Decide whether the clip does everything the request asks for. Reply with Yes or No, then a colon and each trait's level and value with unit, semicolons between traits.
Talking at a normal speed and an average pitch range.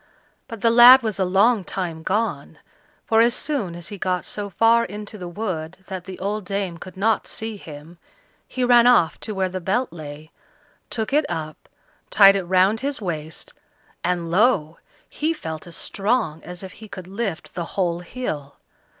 Yes: average, 180 wpm; average, 4.5 semitones